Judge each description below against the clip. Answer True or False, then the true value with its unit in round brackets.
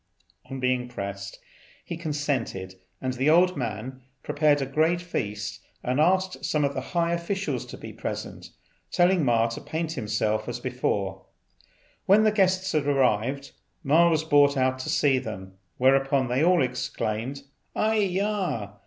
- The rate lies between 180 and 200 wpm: False (155 wpm)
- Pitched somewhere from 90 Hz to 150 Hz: True (140 Hz)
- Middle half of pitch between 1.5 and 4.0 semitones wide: False (5.6 semitones)